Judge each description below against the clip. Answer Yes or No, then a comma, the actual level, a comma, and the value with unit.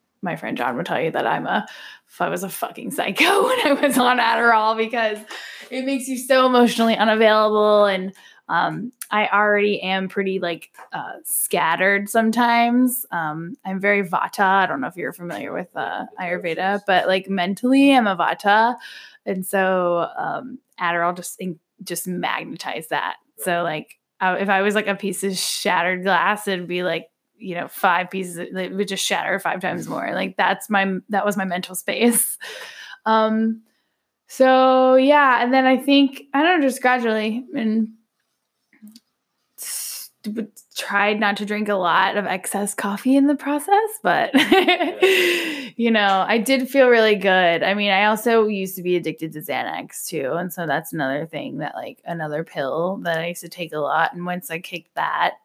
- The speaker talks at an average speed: Yes, average, 175 wpm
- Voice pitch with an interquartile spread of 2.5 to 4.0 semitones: No, average, 4.7 semitones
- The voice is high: Yes, high, 205 Hz